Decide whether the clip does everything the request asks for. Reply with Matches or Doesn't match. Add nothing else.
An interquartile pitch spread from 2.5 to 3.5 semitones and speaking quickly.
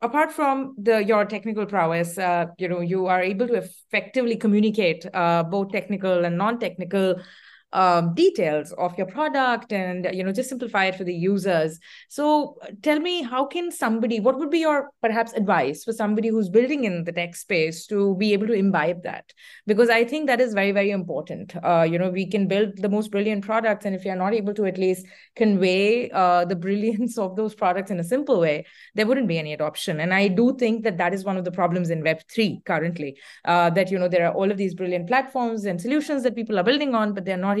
Doesn't match